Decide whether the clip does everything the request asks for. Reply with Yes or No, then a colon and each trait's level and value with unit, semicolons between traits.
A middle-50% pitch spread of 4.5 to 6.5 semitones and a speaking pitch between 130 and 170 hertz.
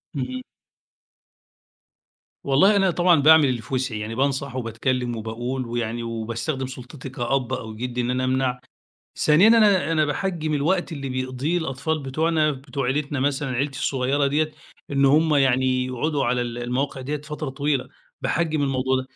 No: average, 3.0 semitones; low, 135 Hz